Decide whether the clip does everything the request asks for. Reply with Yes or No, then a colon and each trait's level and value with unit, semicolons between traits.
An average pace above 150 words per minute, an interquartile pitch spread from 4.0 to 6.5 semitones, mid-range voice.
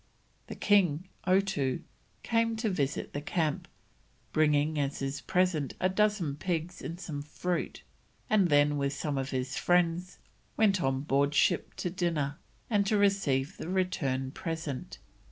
No: average, 145 wpm; average, 4.7 semitones; medium, 160 Hz